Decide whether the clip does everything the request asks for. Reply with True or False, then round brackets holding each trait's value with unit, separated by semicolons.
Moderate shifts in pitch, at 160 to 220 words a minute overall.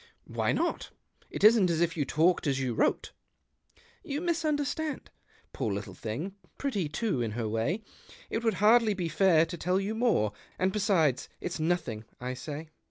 False (8.4 semitones; 175 wpm)